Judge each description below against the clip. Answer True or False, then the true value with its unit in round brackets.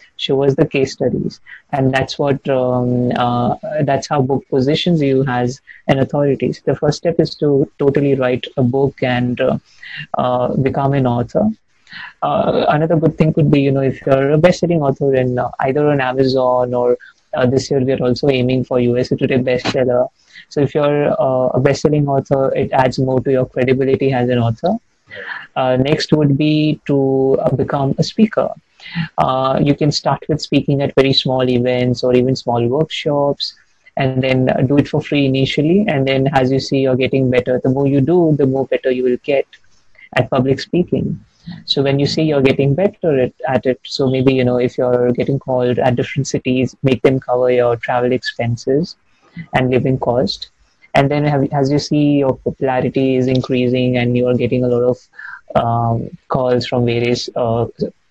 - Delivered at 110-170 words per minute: False (185 wpm)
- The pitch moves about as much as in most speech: False (2.2 semitones)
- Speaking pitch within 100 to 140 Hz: True (135 Hz)